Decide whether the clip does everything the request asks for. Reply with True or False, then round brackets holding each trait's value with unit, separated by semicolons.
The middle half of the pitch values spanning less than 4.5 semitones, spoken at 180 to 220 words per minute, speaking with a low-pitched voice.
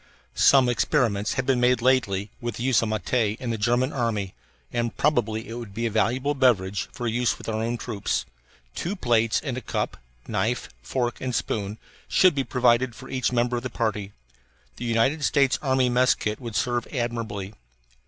True (2.5 semitones; 190 wpm; 120 Hz)